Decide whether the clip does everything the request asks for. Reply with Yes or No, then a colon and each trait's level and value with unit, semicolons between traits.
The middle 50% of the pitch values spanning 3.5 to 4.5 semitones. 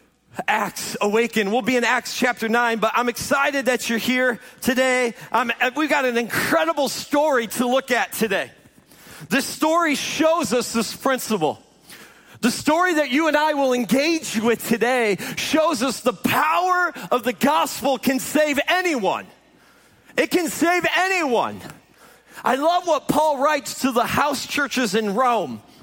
Yes: average, 4.2 semitones